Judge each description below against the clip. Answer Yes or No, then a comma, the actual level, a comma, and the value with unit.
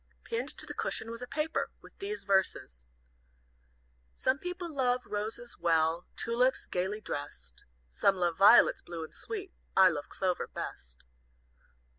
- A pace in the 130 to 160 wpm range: Yes, average, 140 wpm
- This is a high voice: Yes, high, 205 Hz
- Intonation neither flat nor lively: No, wide, 7.5 semitones